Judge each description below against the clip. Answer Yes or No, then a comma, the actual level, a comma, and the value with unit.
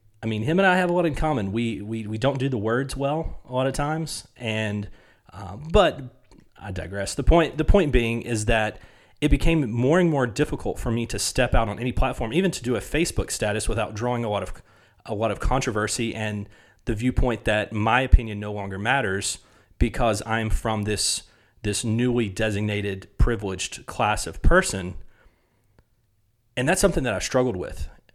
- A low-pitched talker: Yes, low, 115 Hz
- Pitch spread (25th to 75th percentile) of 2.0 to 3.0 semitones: No, average, 3.8 semitones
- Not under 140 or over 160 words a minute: No, average, 190 wpm